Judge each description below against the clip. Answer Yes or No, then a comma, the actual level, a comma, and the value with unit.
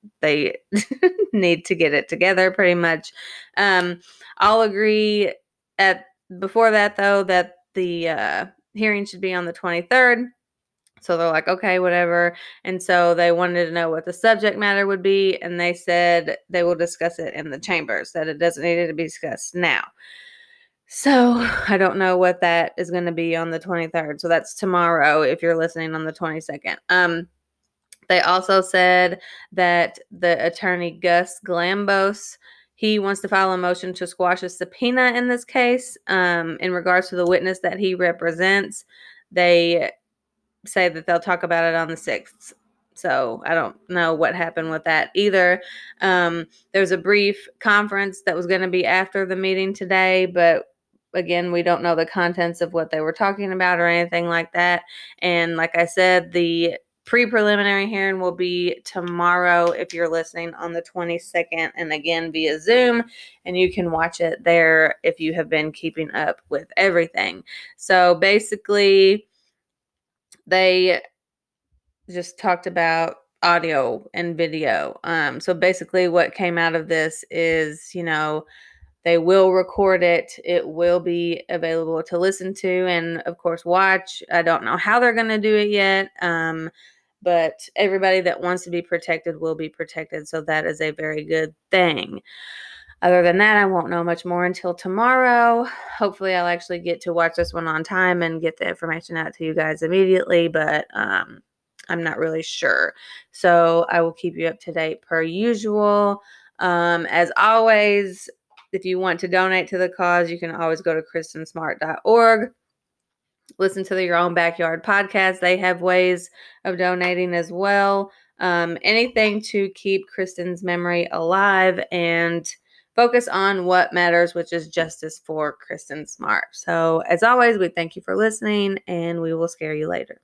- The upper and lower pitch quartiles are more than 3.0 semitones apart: No, narrow, 2.4 semitones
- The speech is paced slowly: No, average, 170 wpm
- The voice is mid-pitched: Yes, medium, 180 Hz